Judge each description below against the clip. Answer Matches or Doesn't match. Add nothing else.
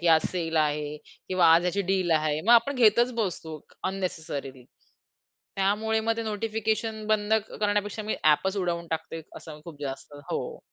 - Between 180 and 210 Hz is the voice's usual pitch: Matches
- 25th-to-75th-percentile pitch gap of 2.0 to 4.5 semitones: Doesn't match